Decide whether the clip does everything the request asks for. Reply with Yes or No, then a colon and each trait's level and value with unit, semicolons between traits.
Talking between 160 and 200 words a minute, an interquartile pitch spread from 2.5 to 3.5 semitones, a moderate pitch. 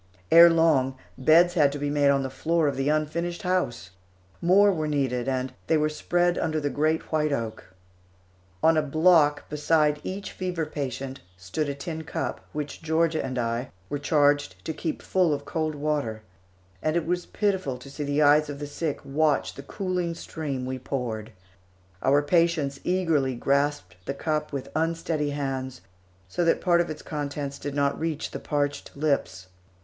Yes: average, 175 wpm; average, 2.9 semitones; medium, 150 Hz